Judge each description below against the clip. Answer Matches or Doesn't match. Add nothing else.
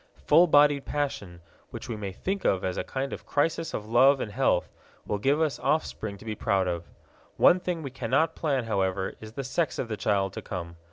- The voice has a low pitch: Matches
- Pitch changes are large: Matches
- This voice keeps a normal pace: Doesn't match